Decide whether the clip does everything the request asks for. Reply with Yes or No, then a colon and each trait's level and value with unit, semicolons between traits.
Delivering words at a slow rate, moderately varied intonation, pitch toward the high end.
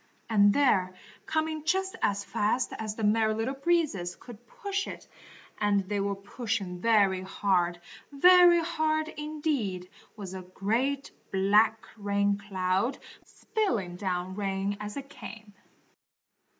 No: slow, 125 wpm; wide, 6.4 semitones; high, 210 Hz